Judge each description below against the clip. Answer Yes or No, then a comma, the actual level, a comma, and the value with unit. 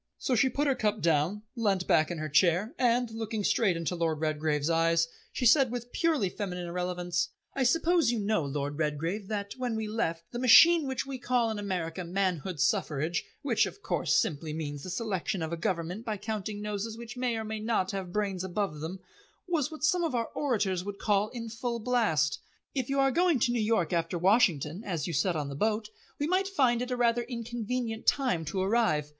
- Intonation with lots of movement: Yes, wide, 6.0 semitones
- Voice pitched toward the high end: Yes, high, 210 Hz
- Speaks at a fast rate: Yes, fast, 210 wpm